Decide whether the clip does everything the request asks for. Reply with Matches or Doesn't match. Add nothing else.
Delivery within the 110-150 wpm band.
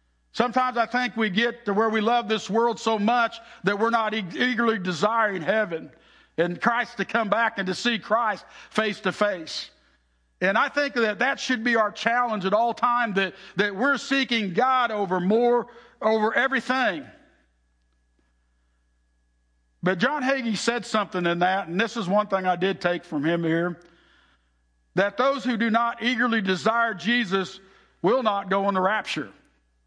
Doesn't match